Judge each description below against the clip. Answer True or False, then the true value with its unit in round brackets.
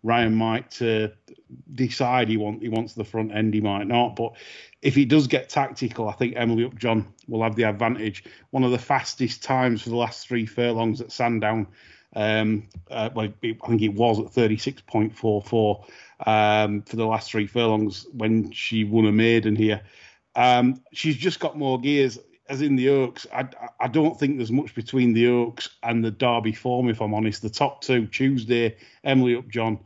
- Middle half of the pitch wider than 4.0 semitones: False (2.4 semitones)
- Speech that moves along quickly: False (185 wpm)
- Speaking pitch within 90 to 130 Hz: True (115 Hz)